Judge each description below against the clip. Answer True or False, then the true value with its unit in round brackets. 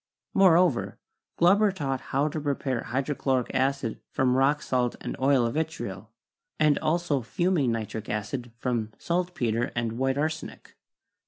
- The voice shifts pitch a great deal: False (4.6 semitones)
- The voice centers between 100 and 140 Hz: True (135 Hz)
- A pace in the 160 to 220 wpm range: False (135 wpm)